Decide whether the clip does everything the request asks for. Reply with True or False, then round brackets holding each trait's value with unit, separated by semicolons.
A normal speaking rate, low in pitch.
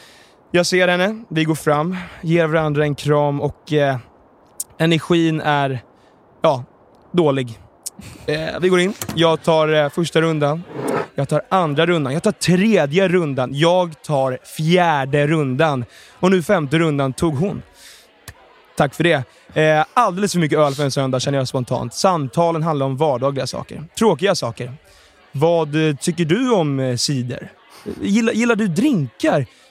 False (150 wpm; 160 Hz)